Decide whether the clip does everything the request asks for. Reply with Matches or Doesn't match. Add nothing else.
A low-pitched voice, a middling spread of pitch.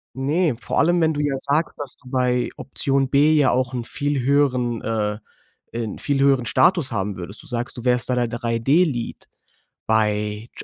Matches